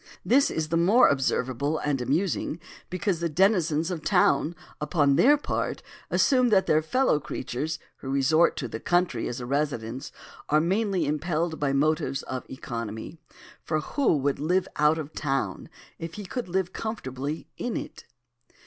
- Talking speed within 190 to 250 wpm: No, average, 160 wpm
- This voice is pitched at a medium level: Yes, medium, 155 Hz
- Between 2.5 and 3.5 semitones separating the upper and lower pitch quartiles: No, average, 4.8 semitones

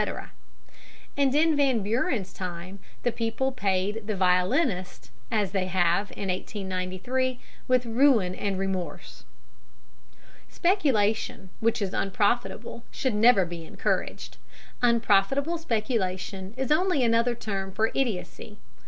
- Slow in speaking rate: Yes, slow, 110 wpm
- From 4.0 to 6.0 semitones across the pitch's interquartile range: Yes, average, 4.9 semitones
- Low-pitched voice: No, high, 215 Hz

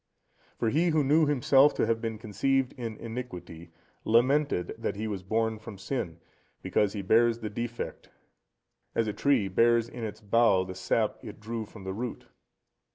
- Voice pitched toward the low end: Yes, low, 115 Hz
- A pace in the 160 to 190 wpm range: Yes, average, 170 wpm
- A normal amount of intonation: Yes, average, 3.1 semitones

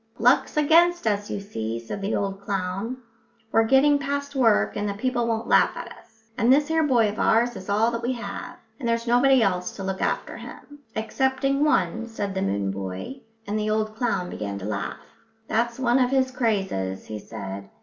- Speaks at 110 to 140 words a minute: No, average, 200 wpm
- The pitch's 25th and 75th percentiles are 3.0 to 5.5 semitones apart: Yes, average, 5.0 semitones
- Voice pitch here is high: Yes, high, 225 Hz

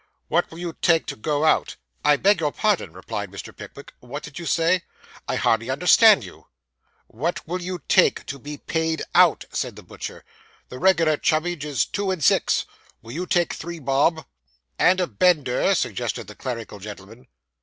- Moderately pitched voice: Yes, medium, 155 Hz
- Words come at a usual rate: Yes, average, 175 wpm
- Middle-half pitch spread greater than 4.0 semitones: Yes, average, 5.1 semitones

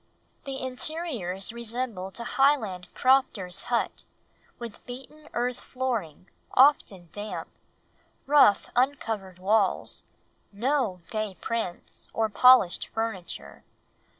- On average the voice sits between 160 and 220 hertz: No, high, 230 Hz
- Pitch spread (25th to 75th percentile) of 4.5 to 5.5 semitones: Yes, average, 5.1 semitones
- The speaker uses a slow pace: Yes, slow, 95 wpm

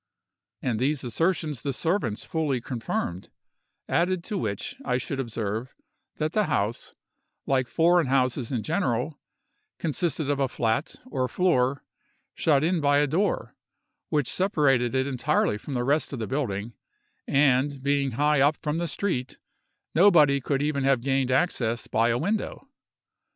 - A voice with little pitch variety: No, average, 4.0 semitones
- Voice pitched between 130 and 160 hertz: Yes, medium, 140 Hz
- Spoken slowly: No, average, 150 wpm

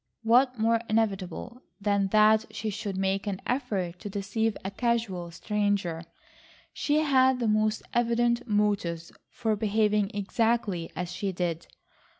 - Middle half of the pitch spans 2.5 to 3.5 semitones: Yes, average, 3.1 semitones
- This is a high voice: Yes, high, 210 Hz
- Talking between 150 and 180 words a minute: No, slow, 135 wpm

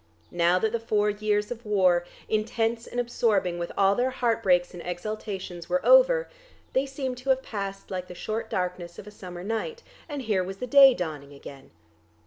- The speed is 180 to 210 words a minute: Yes, average, 185 wpm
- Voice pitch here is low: No, high, 210 Hz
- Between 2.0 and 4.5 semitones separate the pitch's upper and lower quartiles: No, average, 5.0 semitones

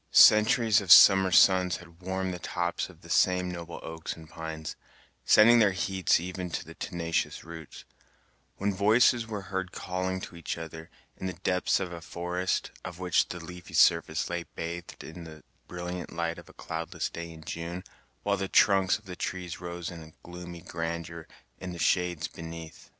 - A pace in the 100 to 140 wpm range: No, average, 175 wpm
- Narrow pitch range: Yes, narrow, 2.0 semitones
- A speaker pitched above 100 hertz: No, very low, 90 Hz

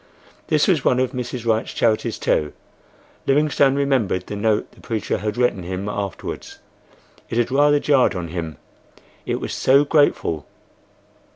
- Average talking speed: Yes, average, 145 wpm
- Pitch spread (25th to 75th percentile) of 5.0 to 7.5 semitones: Yes, wide, 5.5 semitones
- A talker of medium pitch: No, low, 115 Hz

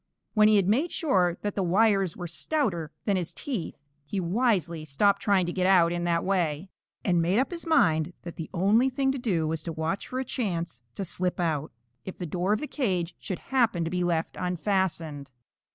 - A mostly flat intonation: No, average, 3.9 semitones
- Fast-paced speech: Yes, fast, 210 wpm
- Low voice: No, medium, 185 Hz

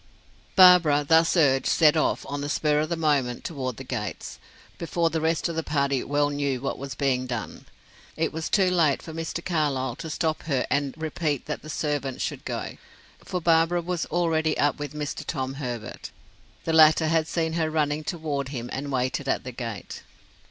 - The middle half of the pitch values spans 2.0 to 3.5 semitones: Yes, average, 2.8 semitones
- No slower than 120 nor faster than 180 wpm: No, average, 190 wpm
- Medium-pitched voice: Yes, medium, 150 Hz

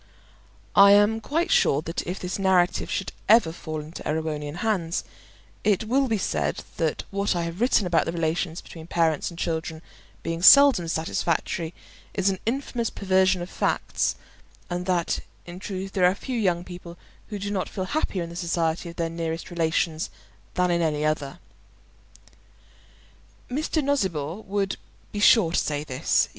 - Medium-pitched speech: Yes, medium, 175 Hz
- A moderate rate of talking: Yes, average, 165 wpm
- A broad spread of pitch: No, average, 3.4 semitones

